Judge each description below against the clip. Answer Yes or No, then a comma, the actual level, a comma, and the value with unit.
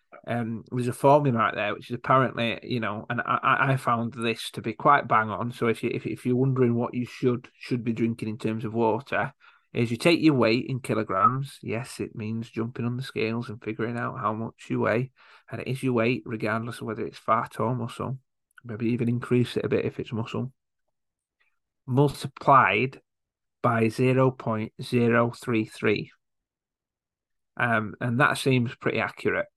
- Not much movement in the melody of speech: Yes, narrow, 2.2 semitones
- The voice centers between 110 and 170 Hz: Yes, low, 120 Hz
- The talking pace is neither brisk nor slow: Yes, average, 190 wpm